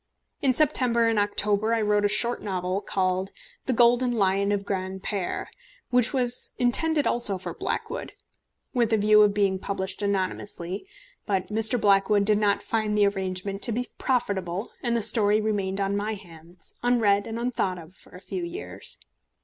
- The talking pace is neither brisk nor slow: Yes, average, 165 wpm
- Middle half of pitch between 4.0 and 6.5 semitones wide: No, average, 3.3 semitones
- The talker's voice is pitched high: Yes, high, 205 Hz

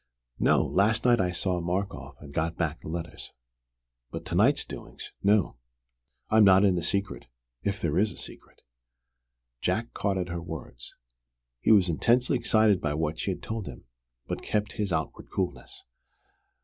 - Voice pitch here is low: Yes, very low, 95 Hz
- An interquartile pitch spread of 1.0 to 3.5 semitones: No, average, 4.1 semitones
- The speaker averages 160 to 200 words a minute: Yes, average, 175 wpm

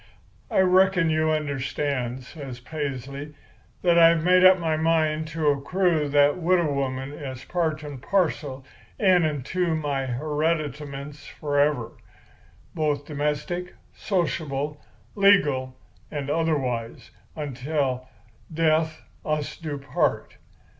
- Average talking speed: No, slow, 110 wpm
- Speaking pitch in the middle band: Yes, medium, 150 Hz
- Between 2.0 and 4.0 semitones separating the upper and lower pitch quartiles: Yes, average, 2.8 semitones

